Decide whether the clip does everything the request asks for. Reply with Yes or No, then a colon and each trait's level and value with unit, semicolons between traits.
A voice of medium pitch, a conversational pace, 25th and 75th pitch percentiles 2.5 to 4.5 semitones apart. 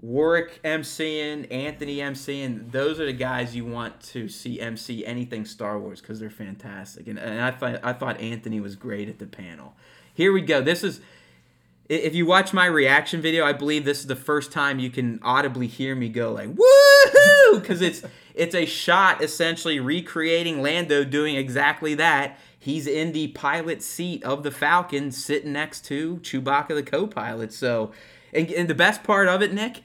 No: medium, 145 Hz; average, 185 wpm; average, 5.3 semitones